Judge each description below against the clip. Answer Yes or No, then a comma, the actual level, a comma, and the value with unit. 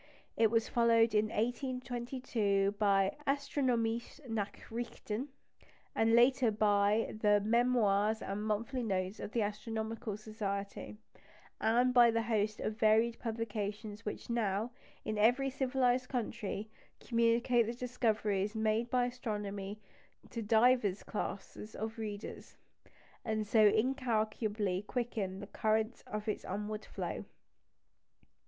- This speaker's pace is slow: Yes, slow, 115 wpm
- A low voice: No, high, 220 Hz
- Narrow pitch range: Yes, narrow, 2.3 semitones